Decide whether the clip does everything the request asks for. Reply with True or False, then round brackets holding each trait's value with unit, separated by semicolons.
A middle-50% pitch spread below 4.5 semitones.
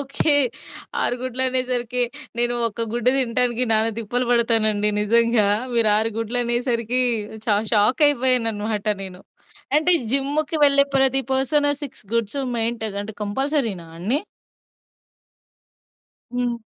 True (2.9 semitones)